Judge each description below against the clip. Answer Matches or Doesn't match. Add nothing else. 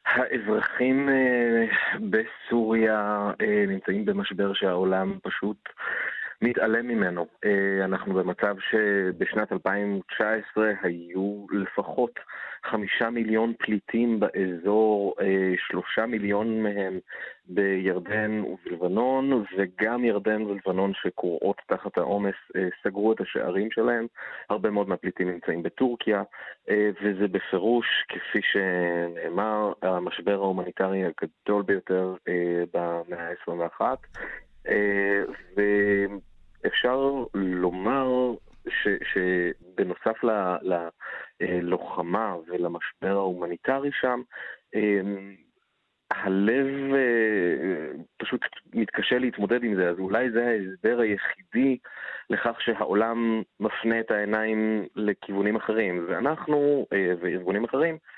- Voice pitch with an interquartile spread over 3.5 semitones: Doesn't match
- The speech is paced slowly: Matches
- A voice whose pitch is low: Matches